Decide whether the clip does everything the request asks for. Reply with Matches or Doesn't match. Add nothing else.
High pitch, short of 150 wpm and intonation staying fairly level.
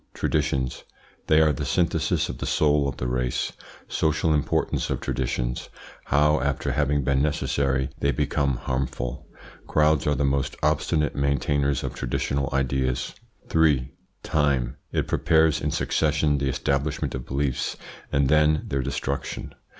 Doesn't match